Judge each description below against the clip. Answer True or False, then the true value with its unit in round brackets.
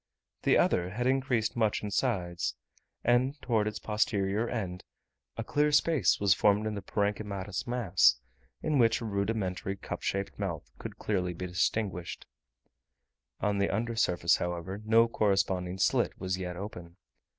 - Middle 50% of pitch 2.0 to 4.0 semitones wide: True (3.7 semitones)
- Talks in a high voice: False (100 Hz)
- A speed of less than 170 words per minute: True (150 wpm)